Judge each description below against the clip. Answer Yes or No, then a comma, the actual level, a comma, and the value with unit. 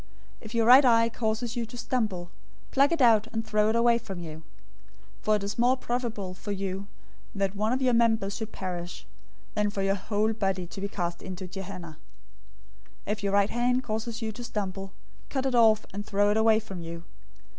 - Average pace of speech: No, fast, 210 wpm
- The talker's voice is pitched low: No, high, 210 Hz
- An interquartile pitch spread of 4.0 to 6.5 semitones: No, average, 3.2 semitones